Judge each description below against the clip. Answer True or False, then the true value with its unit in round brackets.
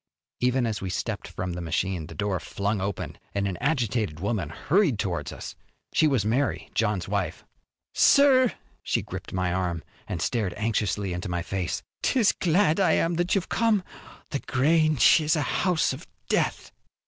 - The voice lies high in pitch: False (110 Hz)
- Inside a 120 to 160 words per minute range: False (170 wpm)